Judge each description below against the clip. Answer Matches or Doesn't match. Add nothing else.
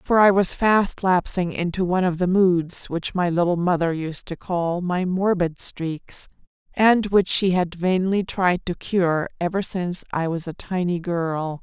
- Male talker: Doesn't match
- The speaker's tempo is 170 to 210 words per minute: Matches